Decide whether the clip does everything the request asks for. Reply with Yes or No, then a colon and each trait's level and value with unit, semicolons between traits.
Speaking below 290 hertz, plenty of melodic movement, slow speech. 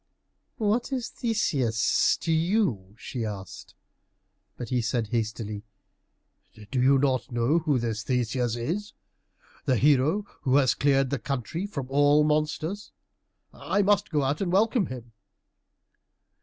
Yes: medium, 140 Hz; wide, 6.0 semitones; slow, 130 wpm